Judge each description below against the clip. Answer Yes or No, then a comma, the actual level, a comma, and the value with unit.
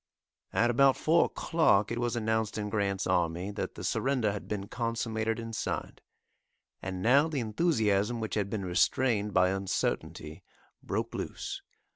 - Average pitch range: Yes, average, 3.4 semitones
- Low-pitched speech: Yes, low, 110 Hz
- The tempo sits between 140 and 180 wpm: Yes, average, 150 wpm